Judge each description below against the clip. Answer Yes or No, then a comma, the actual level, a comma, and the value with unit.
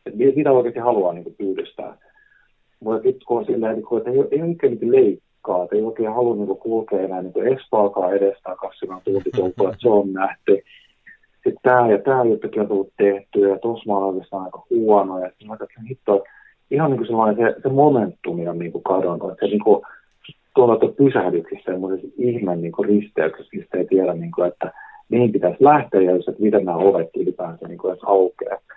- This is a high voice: No, low, 110 Hz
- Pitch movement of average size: No, wide, 6.7 semitones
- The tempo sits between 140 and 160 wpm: Yes, average, 150 wpm